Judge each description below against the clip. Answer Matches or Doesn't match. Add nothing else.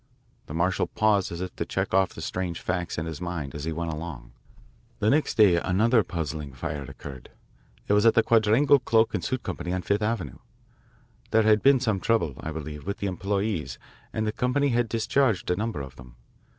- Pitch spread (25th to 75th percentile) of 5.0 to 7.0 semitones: Matches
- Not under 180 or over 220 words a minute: Matches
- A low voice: Matches